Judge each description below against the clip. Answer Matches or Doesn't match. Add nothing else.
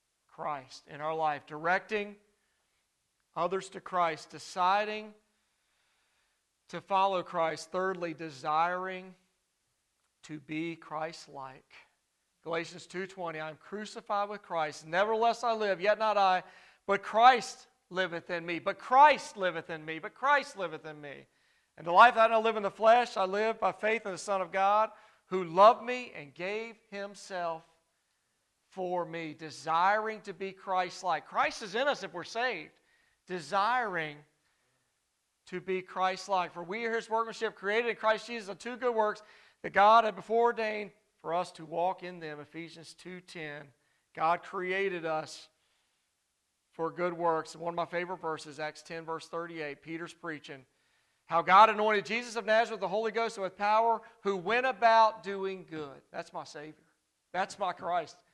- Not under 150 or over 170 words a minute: Matches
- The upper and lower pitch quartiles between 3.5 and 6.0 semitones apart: Matches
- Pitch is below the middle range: Doesn't match